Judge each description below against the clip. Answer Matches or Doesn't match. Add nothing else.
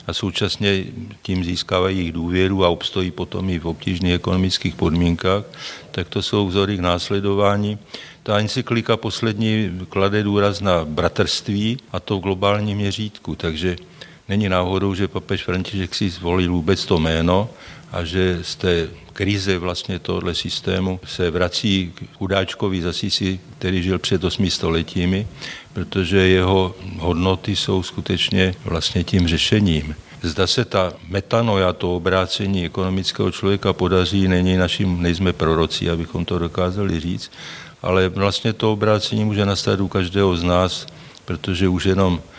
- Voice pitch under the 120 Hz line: Matches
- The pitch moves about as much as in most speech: Doesn't match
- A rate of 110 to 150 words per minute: Matches